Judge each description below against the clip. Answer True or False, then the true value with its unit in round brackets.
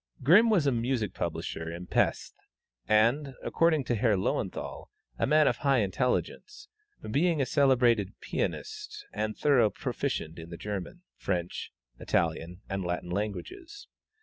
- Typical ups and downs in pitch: False (8.3 semitones)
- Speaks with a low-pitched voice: True (120 Hz)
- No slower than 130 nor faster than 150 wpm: True (140 wpm)